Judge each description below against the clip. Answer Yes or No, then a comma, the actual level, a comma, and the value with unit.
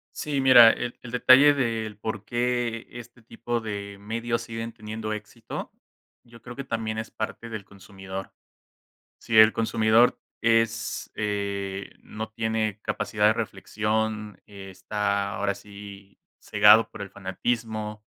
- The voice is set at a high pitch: No, low, 110 Hz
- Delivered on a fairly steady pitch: Yes, narrow, 2.1 semitones